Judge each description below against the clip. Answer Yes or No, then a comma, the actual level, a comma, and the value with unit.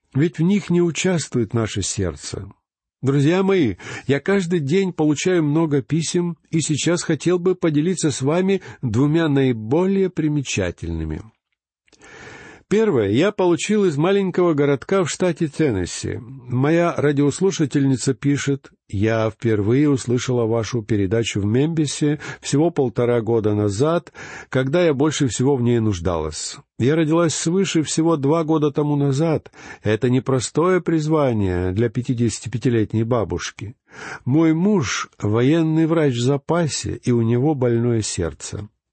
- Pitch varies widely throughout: Yes, wide, 5.7 semitones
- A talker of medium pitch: Yes, medium, 145 Hz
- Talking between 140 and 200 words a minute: No, average, 125 wpm